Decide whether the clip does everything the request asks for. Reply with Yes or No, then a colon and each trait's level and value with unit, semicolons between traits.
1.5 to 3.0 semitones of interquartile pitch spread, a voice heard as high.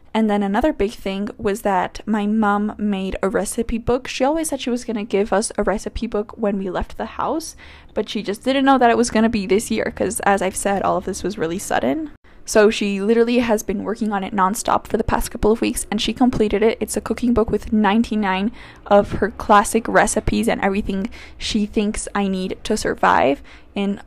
Yes: narrow, 2.5 semitones; high, 210 Hz